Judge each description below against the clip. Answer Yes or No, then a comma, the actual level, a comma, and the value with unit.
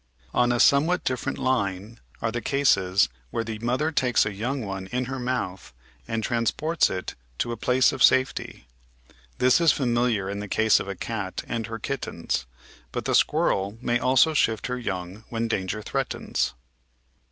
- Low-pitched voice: Yes, low, 115 Hz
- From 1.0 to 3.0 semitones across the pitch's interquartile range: No, average, 4.0 semitones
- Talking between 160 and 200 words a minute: Yes, average, 170 wpm